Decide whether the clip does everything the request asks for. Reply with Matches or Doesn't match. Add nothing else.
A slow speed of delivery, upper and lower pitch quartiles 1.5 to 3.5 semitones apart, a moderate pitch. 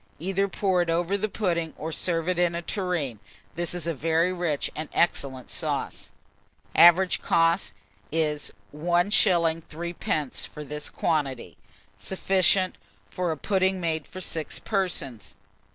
Matches